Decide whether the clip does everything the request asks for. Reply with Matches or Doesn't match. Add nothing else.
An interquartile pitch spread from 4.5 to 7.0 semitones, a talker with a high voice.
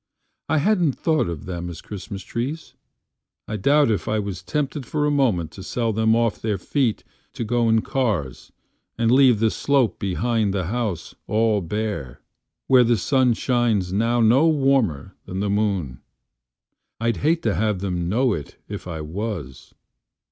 Doesn't match